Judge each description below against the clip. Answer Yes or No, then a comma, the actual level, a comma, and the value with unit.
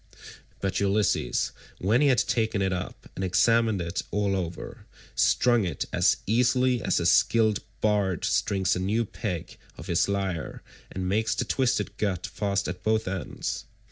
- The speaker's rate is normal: Yes, average, 160 wpm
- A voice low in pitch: Yes, low, 100 Hz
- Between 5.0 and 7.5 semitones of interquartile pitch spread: No, average, 3.1 semitones